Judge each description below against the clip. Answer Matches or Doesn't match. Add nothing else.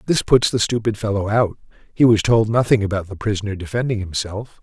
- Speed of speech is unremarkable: Matches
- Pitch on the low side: Matches